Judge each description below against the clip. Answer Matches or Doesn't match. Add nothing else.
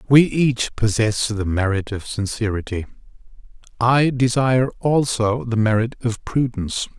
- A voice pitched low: Matches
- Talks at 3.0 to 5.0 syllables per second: Matches